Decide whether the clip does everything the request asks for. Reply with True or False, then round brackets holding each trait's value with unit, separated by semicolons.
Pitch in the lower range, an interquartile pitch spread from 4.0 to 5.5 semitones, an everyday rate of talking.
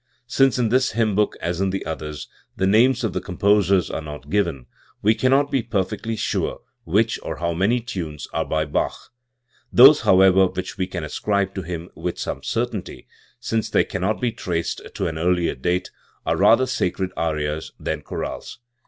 True (95 Hz; 4.9 semitones; 180 wpm)